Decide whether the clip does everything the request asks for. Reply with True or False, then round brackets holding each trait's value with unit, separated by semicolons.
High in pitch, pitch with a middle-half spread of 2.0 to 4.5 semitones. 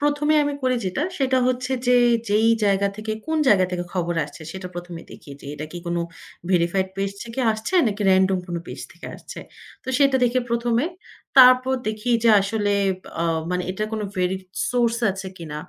False (210 Hz; 5.4 semitones)